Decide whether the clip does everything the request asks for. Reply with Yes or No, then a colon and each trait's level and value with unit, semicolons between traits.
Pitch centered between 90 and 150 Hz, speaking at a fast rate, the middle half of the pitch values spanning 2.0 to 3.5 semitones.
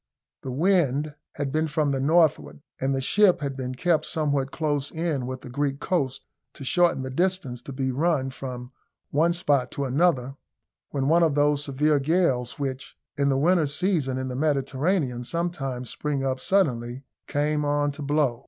No: medium, 140 Hz; average, 175 wpm; average, 3.1 semitones